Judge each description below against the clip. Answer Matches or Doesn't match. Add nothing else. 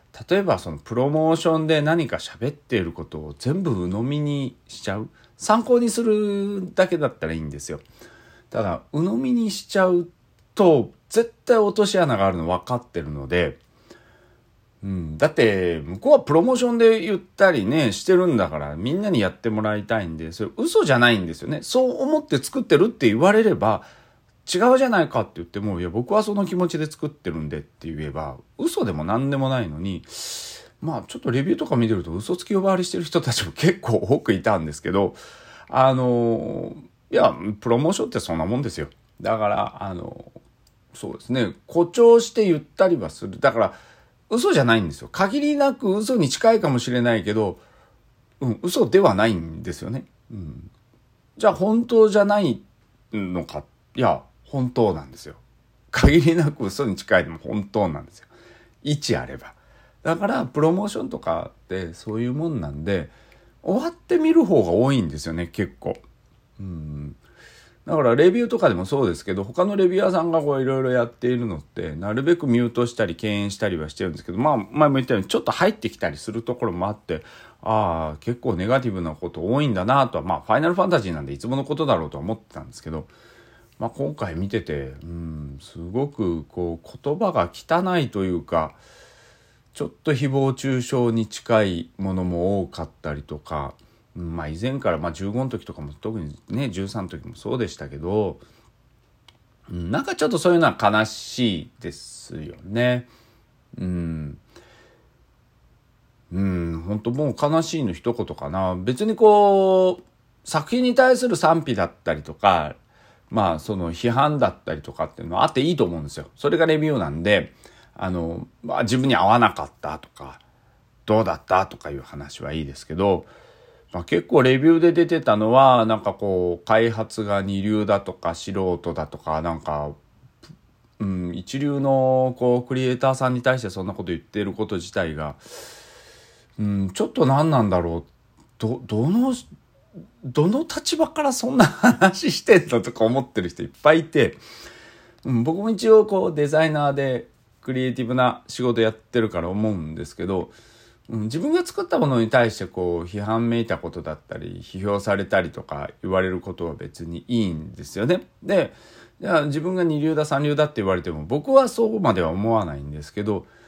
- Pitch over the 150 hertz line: Doesn't match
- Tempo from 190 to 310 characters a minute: Doesn't match